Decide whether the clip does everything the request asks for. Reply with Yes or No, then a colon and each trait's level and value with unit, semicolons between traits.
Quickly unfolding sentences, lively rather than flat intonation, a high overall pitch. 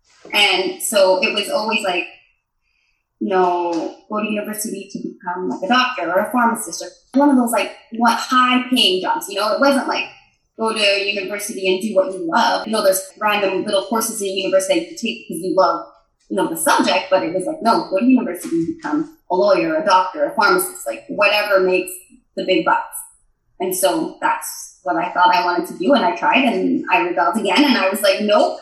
Yes: fast, 215 wpm; wide, 7.4 semitones; high, 220 Hz